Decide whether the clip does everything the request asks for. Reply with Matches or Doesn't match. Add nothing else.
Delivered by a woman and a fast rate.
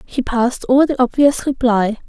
Doesn't match